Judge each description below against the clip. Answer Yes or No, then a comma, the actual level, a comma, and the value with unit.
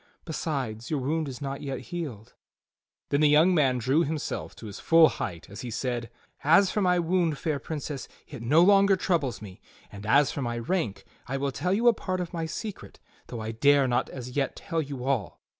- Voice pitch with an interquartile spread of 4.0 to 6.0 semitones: Yes, average, 5.1 semitones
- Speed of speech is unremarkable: No, fast, 210 wpm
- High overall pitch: No, medium, 140 Hz